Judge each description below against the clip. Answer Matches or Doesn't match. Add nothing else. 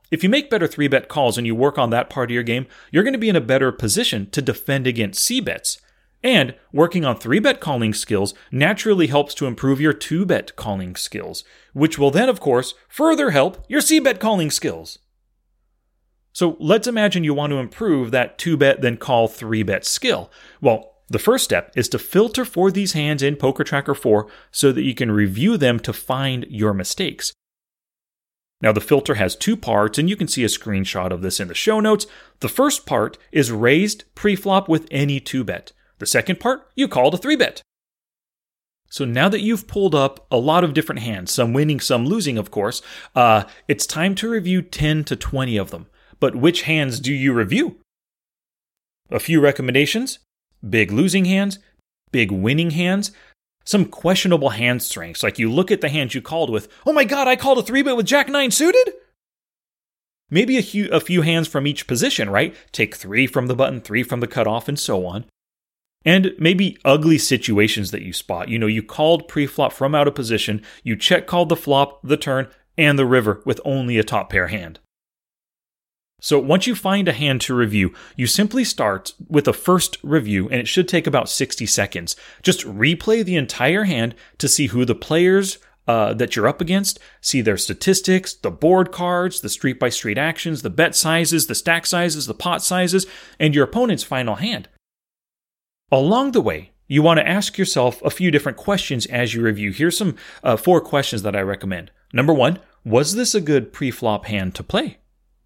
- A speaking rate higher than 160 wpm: Matches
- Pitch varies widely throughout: Matches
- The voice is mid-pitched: Matches